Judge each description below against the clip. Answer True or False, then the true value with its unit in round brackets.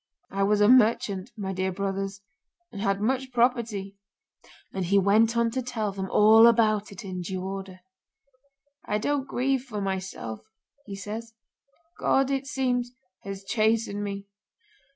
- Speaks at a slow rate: False (150 wpm)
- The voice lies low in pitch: False (210 Hz)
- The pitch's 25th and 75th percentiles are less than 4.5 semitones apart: True (3.2 semitones)